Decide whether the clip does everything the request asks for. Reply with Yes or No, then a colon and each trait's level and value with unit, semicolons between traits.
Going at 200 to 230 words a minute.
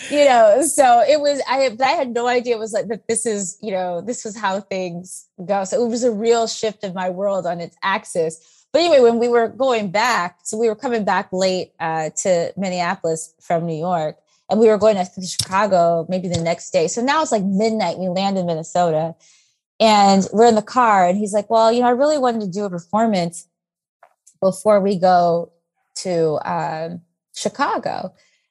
Yes: fast, 205 wpm